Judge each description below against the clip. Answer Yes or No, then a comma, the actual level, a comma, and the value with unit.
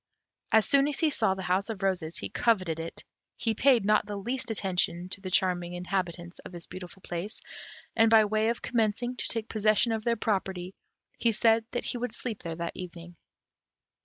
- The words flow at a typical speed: Yes, average, 195 wpm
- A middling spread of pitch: Yes, average, 4.0 semitones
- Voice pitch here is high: Yes, high, 205 Hz